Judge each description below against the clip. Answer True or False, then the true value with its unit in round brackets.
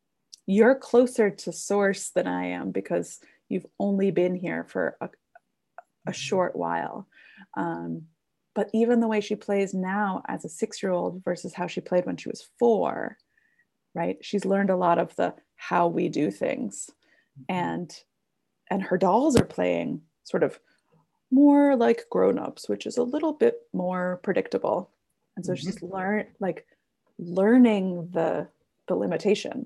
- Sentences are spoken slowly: False (155 wpm)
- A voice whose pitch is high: True (195 Hz)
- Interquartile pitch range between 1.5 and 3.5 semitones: False (4.4 semitones)